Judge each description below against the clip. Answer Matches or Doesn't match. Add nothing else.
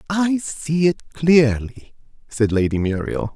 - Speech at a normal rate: Doesn't match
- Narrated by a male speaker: Matches